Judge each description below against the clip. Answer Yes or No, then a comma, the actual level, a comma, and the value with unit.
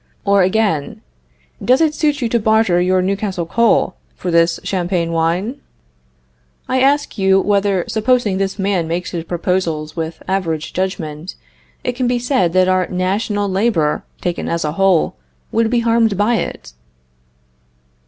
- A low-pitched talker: No, high, 190 Hz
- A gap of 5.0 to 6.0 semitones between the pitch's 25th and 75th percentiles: No, average, 4.3 semitones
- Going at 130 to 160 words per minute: Yes, average, 150 wpm